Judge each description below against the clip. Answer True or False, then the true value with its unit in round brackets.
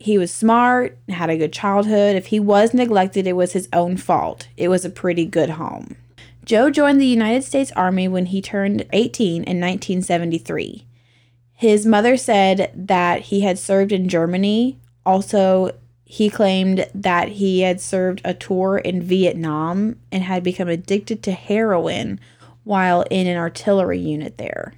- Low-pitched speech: False (190 Hz)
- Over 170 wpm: False (160 wpm)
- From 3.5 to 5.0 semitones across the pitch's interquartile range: False (2.8 semitones)